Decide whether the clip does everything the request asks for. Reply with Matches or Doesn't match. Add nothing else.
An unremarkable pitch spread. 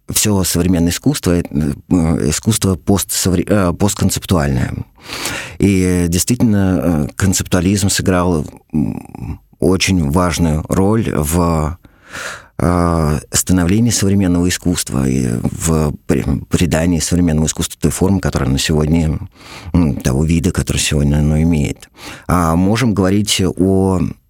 Matches